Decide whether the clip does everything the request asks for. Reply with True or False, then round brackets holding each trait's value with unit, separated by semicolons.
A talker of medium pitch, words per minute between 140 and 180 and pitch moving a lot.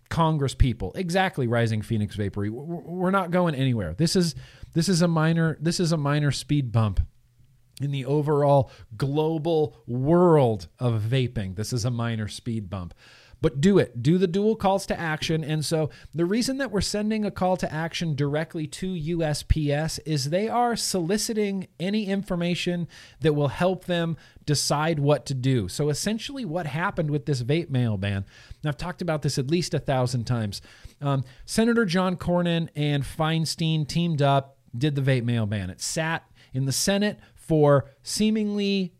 True (150 Hz; 170 wpm; 5.7 semitones)